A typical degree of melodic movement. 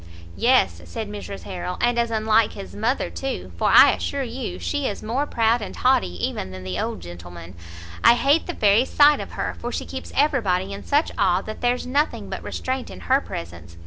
No: wide, 6.4 semitones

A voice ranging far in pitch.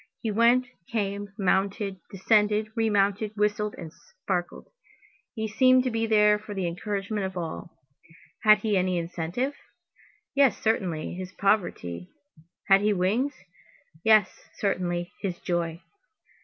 No: average, 3.1 semitones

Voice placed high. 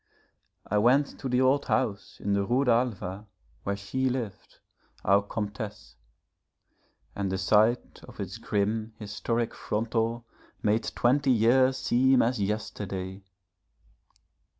No: low, 110 Hz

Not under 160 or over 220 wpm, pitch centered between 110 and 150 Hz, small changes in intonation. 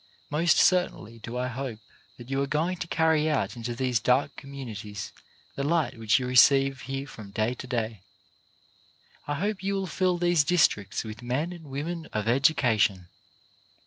No: average, 170 wpm; low, 135 Hz; wide, 5.5 semitones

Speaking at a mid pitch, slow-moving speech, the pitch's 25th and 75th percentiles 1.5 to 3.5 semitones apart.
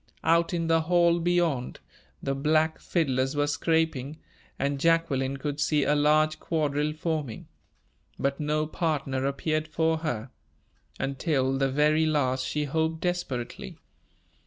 Yes: medium, 150 Hz; slow, 130 wpm; average, 2.8 semitones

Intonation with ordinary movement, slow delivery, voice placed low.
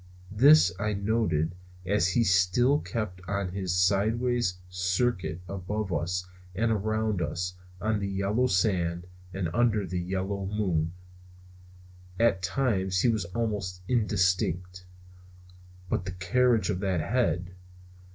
Yes: average, 3.2 semitones; slow, 125 wpm; very low, 95 Hz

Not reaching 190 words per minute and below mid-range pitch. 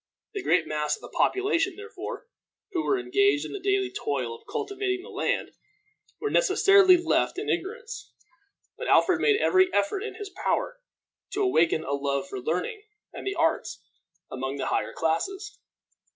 No: average, 165 wpm; very high, 375 Hz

